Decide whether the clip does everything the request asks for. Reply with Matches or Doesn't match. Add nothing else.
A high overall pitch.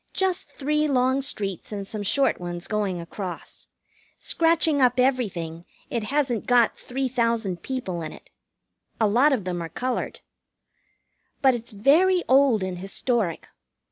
Matches